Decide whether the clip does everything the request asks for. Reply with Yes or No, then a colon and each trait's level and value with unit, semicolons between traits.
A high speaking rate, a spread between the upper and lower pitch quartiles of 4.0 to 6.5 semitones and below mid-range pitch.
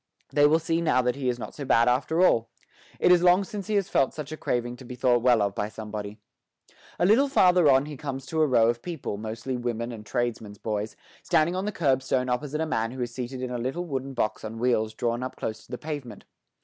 Yes: fast, 250 wpm; average, 4.8 semitones; low, 130 Hz